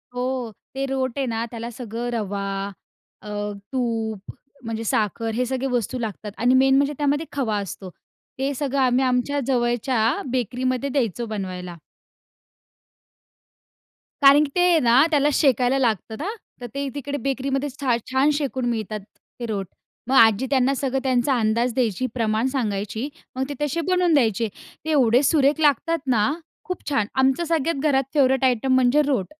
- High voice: Yes, very high, 255 Hz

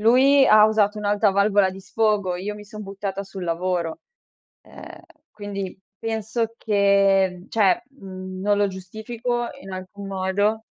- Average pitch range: No, narrow, 2.2 semitones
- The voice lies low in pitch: No, high, 200 Hz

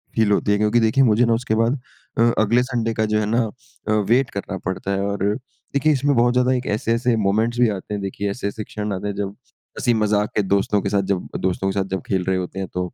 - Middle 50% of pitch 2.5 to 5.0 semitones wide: Yes, average, 3.1 semitones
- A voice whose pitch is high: No, low, 105 Hz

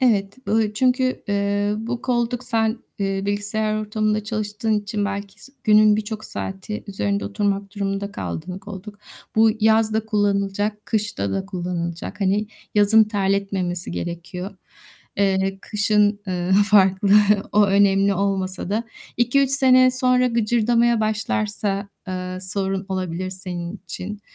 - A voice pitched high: Yes, high, 205 Hz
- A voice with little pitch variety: Yes, narrow, 2.0 semitones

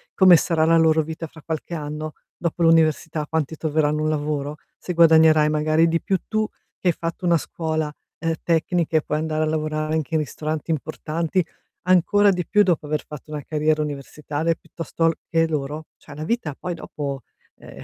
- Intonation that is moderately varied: No, narrow, 1.5 semitones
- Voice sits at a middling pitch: Yes, medium, 155 Hz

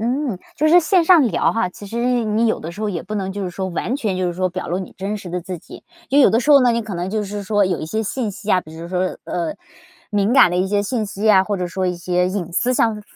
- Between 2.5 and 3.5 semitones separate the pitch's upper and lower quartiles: No, average, 3.9 semitones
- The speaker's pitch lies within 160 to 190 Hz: No, high, 205 Hz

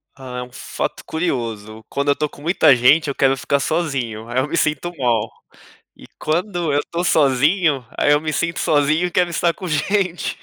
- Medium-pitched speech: Yes, medium, 145 Hz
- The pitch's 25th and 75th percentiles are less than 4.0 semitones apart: No, average, 4.4 semitones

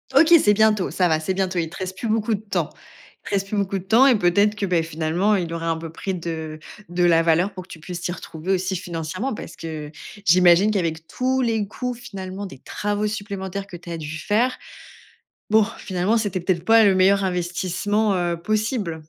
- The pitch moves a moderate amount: Yes, average, 3.5 semitones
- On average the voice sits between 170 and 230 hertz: Yes, medium, 185 Hz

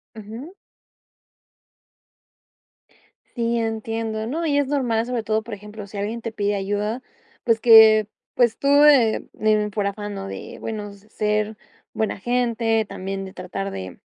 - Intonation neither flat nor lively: No, narrow, 2.1 semitones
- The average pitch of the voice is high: Yes, high, 220 Hz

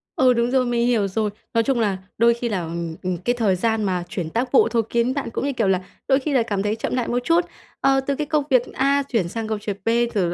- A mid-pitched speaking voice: No, high, 235 Hz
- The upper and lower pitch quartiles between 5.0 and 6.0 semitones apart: No, average, 4.3 semitones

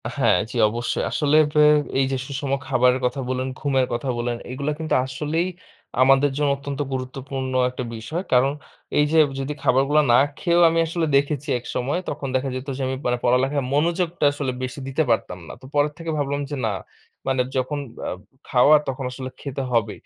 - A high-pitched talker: No, low, 135 Hz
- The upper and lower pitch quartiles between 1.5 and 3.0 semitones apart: Yes, narrow, 2.5 semitones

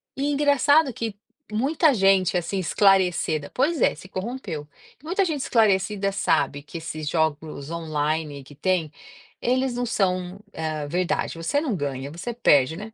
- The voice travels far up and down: Yes, wide, 7.4 semitones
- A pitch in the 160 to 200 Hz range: Yes, medium, 185 Hz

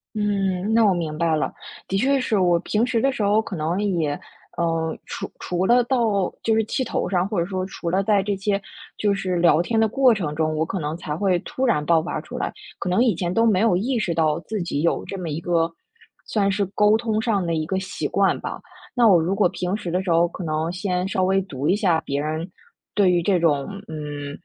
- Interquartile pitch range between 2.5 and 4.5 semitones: Yes, average, 3.9 semitones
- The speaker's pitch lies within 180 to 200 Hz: Yes, medium, 185 Hz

